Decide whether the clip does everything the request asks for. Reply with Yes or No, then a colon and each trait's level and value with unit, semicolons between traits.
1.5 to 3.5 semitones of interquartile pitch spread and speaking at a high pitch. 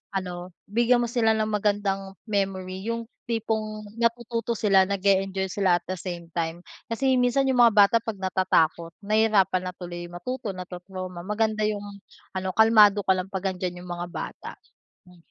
Yes: average, 3.2 semitones; high, 200 Hz